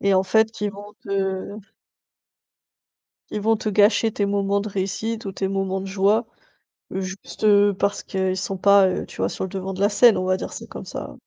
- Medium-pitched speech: No, high, 200 Hz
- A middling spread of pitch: No, narrow, 1.4 semitones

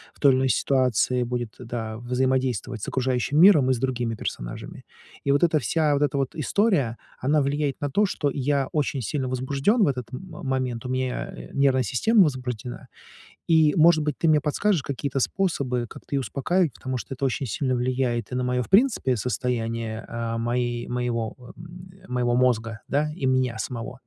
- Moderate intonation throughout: Yes, average, 3.0 semitones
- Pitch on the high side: No, low, 130 Hz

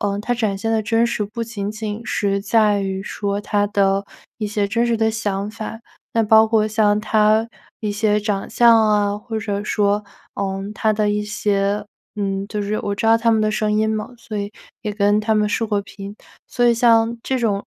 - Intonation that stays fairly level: Yes, narrow, 1.6 semitones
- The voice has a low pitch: No, high, 210 Hz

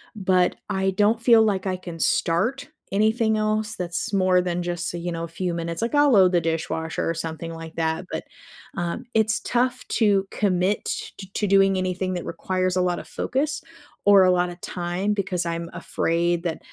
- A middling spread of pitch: Yes, average, 3.2 semitones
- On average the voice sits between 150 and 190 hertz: Yes, medium, 185 Hz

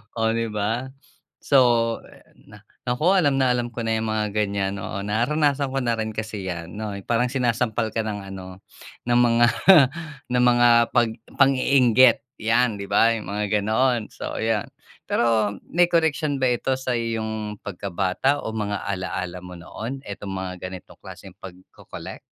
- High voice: No, low, 115 Hz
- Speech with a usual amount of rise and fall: Yes, average, 3.4 semitones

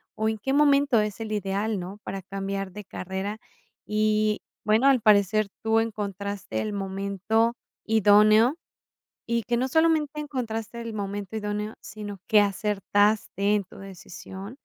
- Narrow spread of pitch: Yes, narrow, 2.1 semitones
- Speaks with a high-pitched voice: Yes, high, 210 Hz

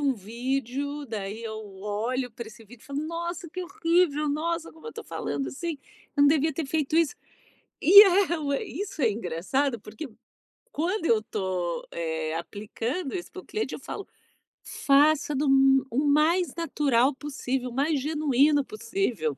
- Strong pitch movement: Yes, wide, 5.7 semitones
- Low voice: No, very high, 280 Hz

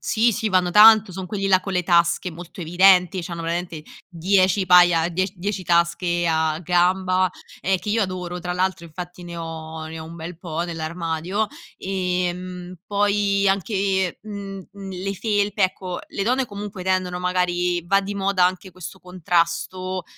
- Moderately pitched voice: Yes, medium, 180 Hz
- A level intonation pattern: Yes, narrow, 2.1 semitones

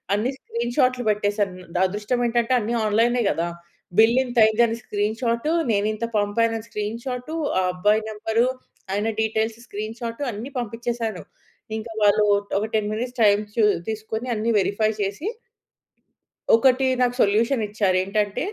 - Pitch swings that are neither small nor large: No, narrow, 2.3 semitones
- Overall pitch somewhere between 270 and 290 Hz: No, high, 220 Hz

